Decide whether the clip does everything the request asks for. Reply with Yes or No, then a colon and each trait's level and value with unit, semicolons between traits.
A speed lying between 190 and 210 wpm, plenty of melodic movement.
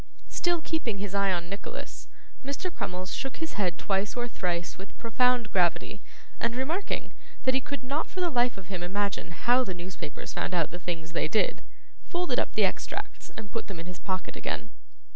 Yes: average, 195 wpm; wide, 6.2 semitones